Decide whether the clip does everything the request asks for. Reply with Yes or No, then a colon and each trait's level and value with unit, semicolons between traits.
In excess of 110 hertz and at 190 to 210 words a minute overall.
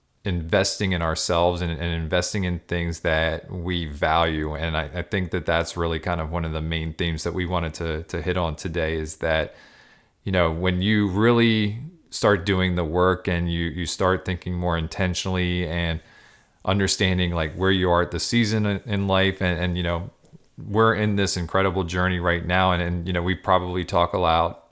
No: very low, 90 Hz; average, 200 wpm